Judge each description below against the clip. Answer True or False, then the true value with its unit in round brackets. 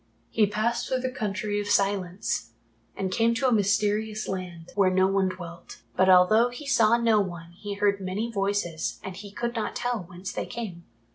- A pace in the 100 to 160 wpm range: False (190 wpm)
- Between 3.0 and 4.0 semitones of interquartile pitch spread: True (3.3 semitones)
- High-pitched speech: True (205 Hz)